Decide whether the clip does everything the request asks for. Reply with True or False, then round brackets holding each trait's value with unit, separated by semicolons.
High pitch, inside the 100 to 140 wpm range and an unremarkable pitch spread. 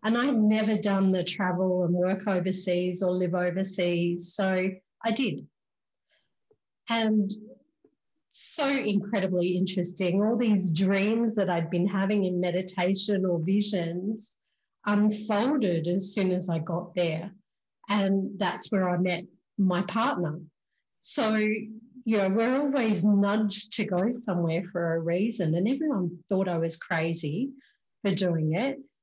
True (195 Hz; 135 wpm; 3.2 semitones)